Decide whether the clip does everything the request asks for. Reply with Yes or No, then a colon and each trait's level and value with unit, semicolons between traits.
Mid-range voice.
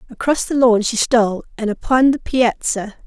No: high, 235 Hz